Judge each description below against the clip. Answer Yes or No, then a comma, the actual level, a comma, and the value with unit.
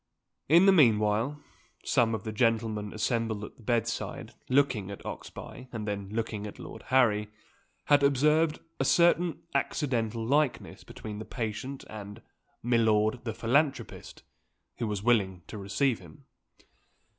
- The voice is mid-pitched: No, low, 115 Hz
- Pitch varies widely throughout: No, average, 4.2 semitones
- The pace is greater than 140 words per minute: No, slow, 135 wpm